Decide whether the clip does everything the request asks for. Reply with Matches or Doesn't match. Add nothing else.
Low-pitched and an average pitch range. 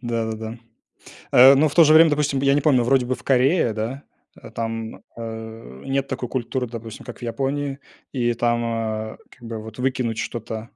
Matches